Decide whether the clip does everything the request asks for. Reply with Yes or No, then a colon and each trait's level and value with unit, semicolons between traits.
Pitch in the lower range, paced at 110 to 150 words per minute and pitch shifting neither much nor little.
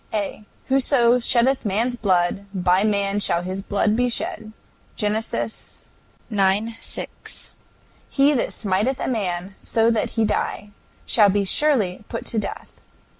No: high, 215 Hz; slow, 135 wpm; average, 3.1 semitones